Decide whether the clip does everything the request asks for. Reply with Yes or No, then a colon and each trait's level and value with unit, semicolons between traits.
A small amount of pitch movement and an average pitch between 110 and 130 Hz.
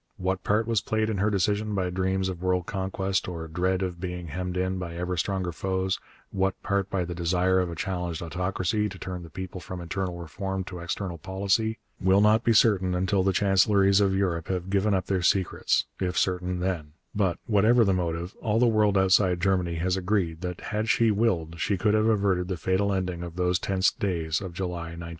No: narrow, 1.8 semitones; very low, 95 Hz